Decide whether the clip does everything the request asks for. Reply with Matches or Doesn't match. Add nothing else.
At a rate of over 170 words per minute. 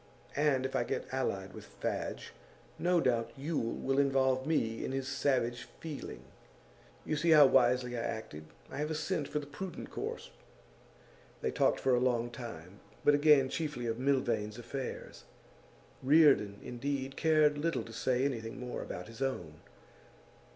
Doesn't match